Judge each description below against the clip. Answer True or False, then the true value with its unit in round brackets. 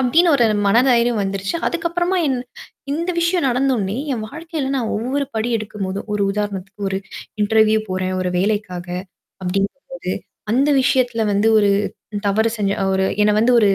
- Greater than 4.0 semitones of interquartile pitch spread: True (5.1 semitones)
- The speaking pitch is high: True (220 Hz)